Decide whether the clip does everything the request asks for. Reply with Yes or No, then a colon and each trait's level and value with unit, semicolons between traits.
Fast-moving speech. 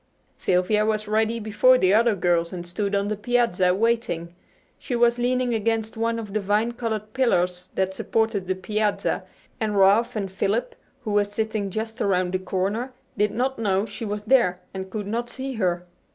No: average, 180 wpm